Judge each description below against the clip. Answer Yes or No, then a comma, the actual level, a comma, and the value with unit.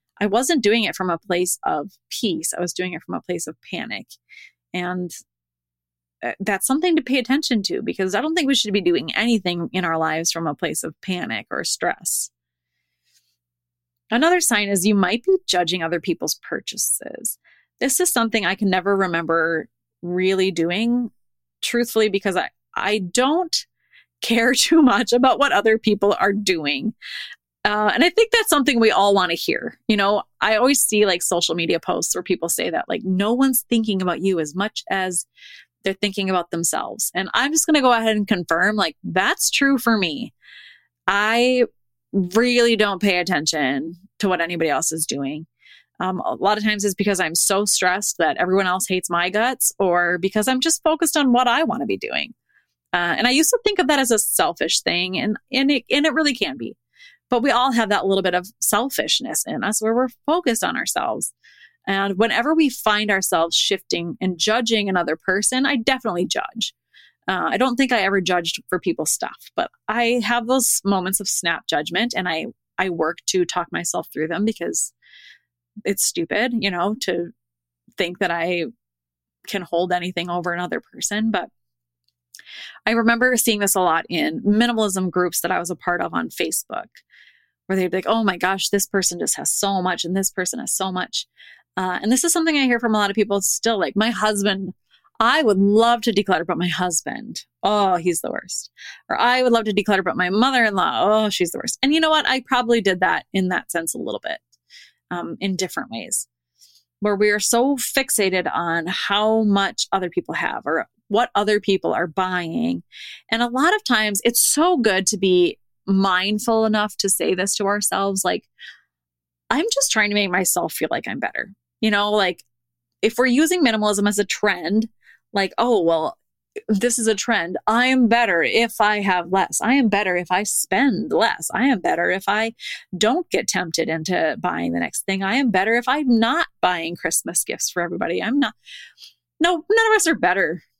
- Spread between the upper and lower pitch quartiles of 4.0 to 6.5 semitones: Yes, average, 4.8 semitones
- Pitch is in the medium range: No, high, 200 Hz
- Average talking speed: Yes, average, 195 wpm